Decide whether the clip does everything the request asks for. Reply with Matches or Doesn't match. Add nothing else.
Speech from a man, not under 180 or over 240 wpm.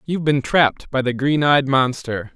Matches